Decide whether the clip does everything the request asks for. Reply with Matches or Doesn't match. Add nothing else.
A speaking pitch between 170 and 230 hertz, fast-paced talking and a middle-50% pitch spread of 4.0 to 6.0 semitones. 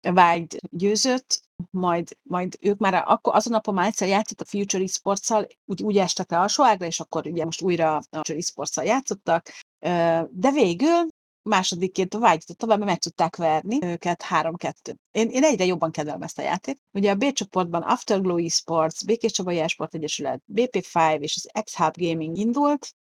Matches